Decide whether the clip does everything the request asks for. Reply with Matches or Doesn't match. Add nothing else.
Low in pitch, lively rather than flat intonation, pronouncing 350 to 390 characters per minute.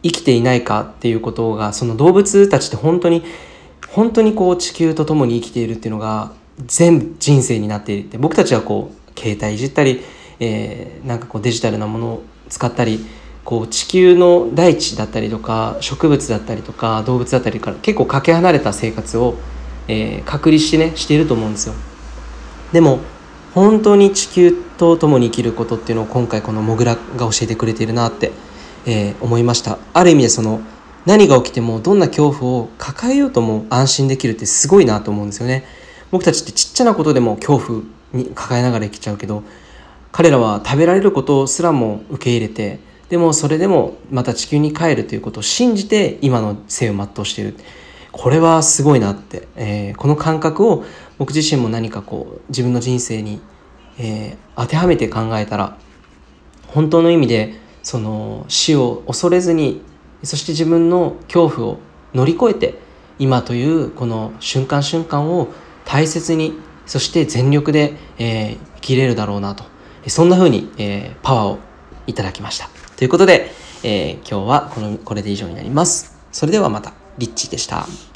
Matches